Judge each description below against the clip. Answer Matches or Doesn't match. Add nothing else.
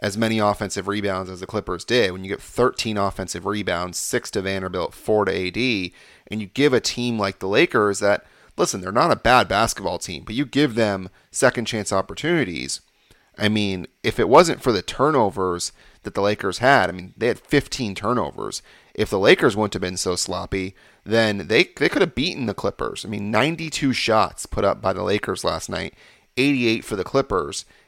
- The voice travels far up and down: Doesn't match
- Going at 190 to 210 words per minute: Matches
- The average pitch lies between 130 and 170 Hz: Doesn't match